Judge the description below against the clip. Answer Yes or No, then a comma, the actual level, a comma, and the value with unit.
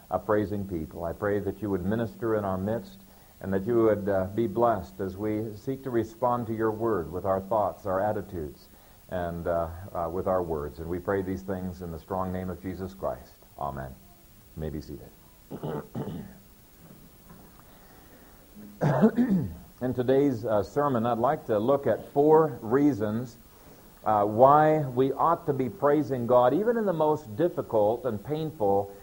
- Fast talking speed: No, average, 165 wpm